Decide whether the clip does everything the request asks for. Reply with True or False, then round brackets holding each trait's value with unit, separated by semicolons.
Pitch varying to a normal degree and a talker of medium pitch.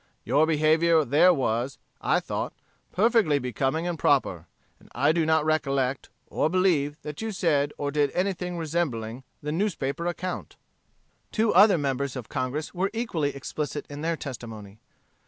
True (3.9 semitones; 150 Hz)